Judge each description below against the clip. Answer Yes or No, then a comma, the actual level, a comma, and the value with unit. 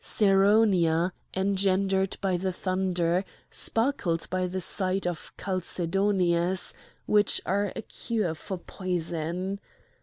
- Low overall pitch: No, medium, 185 Hz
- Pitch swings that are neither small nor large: No, narrow, 2.0 semitones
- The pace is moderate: No, slow, 100 wpm